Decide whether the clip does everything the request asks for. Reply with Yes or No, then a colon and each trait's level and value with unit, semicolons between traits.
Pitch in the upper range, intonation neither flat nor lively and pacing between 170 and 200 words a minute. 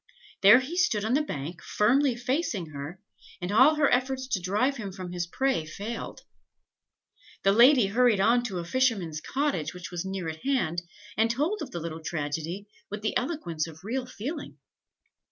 No: high, 210 Hz; wide, 6.9 semitones; average, 175 wpm